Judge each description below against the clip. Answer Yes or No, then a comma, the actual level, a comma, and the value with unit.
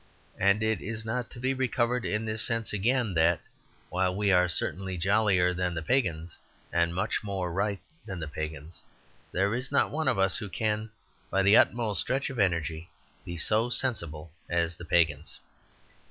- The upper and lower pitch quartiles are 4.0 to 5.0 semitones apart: Yes, average, 4.5 semitones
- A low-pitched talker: Yes, very low, 95 Hz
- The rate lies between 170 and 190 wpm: Yes, average, 175 wpm